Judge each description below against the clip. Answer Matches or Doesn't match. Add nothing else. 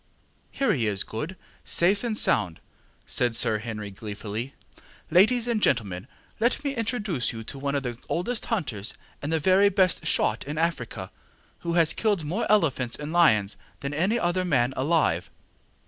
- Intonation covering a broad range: Matches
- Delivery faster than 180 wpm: Doesn't match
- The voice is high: Doesn't match